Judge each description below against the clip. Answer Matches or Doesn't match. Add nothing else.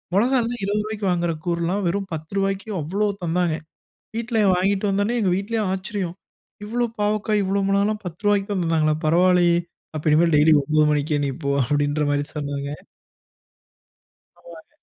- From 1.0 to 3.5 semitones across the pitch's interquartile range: Doesn't match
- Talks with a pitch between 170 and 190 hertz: Matches